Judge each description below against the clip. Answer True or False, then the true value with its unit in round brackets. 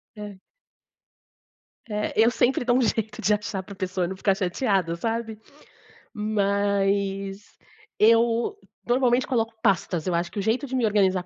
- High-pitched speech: True (210 Hz)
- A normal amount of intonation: True (3.0 semitones)